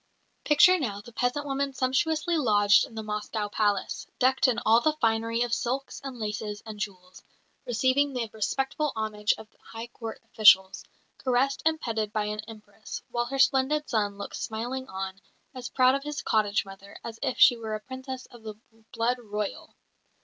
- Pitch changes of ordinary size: Yes, average, 3.8 semitones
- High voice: Yes, high, 230 Hz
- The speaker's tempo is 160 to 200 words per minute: Yes, average, 175 wpm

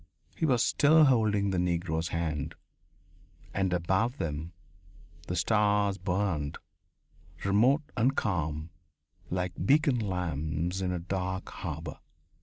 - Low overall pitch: Yes, very low, 95 Hz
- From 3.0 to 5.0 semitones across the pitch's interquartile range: Yes, average, 4.0 semitones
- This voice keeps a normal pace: No, slow, 110 wpm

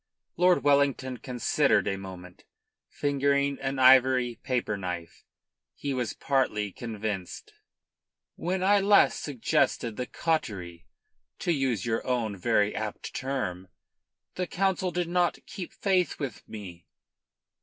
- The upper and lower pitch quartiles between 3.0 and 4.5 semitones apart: No, wide, 5.6 semitones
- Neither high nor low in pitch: No, low, 130 Hz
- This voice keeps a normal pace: No, slow, 120 wpm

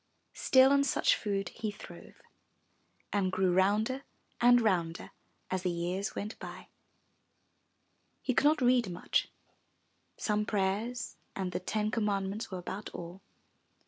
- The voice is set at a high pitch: Yes, high, 205 Hz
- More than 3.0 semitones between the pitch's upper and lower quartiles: Yes, average, 3.7 semitones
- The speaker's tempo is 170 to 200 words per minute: No, average, 140 wpm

